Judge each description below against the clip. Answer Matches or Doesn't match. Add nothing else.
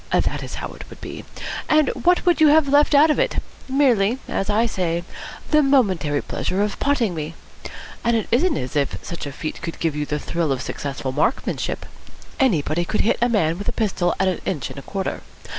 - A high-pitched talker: Matches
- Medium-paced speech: Doesn't match